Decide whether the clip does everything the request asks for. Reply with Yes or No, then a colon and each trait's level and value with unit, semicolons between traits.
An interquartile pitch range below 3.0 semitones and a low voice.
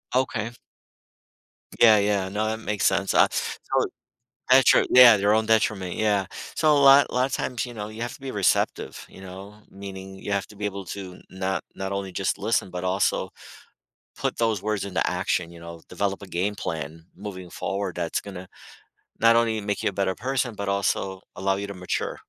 Yes: narrow, 2.6 semitones; low, 100 Hz